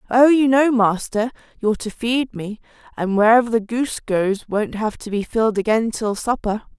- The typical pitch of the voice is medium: No, high, 225 Hz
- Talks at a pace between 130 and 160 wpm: No, average, 185 wpm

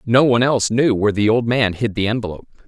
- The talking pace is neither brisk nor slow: No, fast, 245 wpm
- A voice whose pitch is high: No, low, 115 Hz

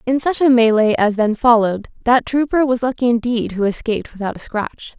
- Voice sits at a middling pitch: No, high, 235 Hz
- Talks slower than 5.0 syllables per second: No, 5.6 syllables/s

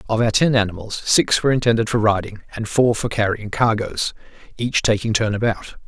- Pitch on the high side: No, low, 110 Hz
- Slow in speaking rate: No, average, 185 wpm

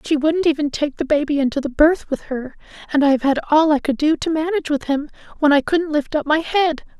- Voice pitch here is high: Yes, very high, 295 Hz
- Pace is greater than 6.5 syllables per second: No, 5.8 syllables/s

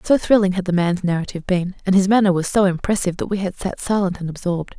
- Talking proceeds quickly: Yes, fast, 250 wpm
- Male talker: No, female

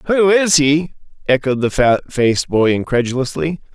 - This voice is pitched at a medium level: Yes, medium, 145 Hz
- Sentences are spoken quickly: No, average, 145 wpm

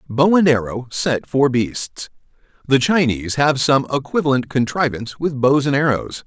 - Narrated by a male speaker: Yes, male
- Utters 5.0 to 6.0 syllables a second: No, 4.8 syllables/s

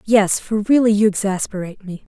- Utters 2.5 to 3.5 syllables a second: No, 5.6 syllables/s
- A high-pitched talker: Yes, high, 205 Hz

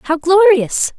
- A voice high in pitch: Yes, very high, 315 Hz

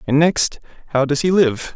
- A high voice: No, medium, 150 Hz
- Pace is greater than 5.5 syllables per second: No, 4.6 syllables/s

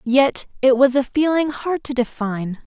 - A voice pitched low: No, very high, 260 Hz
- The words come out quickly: No, average, 175 wpm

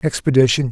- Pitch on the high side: No, low, 130 Hz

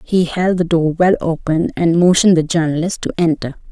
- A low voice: No, medium, 170 Hz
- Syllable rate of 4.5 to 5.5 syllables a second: Yes, 5.3 syllables/s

